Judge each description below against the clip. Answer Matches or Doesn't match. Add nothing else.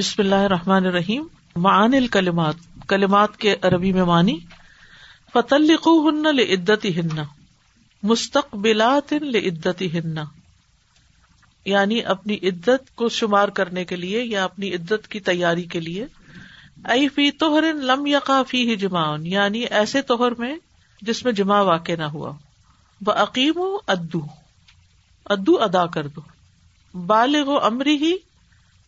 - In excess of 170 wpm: Doesn't match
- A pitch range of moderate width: Doesn't match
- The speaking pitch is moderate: Doesn't match